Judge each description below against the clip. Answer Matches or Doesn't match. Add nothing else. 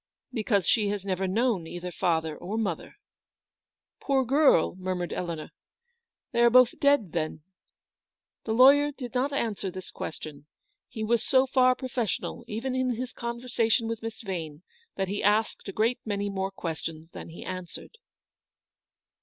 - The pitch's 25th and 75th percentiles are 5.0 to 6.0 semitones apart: Matches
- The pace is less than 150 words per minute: Doesn't match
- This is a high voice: Matches